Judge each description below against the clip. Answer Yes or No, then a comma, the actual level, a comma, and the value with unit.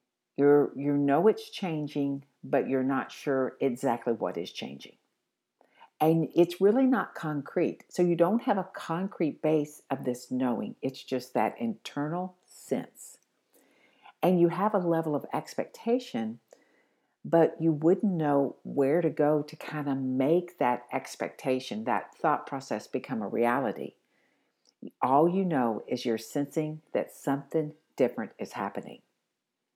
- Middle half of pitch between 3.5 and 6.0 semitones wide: Yes, average, 4.4 semitones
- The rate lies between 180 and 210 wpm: No, average, 140 wpm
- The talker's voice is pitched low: No, medium, 150 Hz